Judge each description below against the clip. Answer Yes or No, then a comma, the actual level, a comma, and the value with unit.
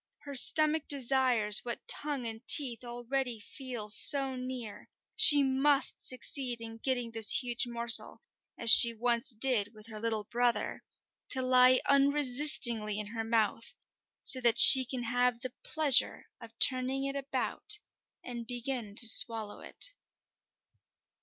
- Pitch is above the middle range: Yes, high, 245 Hz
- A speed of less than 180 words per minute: Yes, average, 140 wpm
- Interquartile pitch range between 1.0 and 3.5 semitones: Yes, average, 2.7 semitones